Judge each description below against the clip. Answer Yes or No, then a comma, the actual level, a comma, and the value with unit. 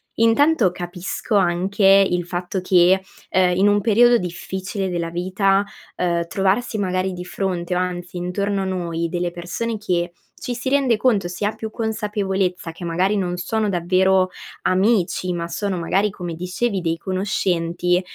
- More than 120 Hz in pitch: Yes, medium, 185 Hz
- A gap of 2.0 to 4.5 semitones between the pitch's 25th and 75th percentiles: Yes, narrow, 2.4 semitones